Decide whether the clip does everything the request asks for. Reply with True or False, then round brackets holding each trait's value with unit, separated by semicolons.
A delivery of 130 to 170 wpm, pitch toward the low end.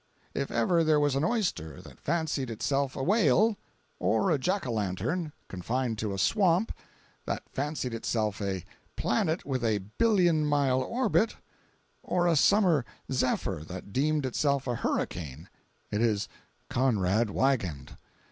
True (140 wpm; 130 Hz)